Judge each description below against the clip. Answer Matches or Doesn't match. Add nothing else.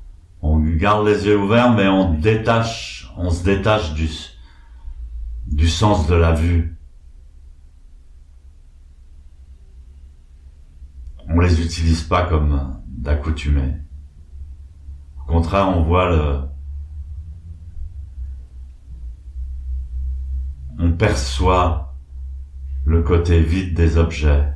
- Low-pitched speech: Matches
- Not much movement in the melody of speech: Doesn't match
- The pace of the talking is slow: Matches